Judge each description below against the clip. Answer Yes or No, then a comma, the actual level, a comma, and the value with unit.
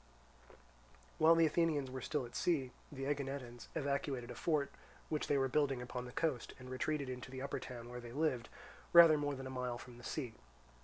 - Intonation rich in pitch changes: No, average, 3.1 semitones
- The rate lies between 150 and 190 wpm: No, average, 200 wpm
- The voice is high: No, low, 135 Hz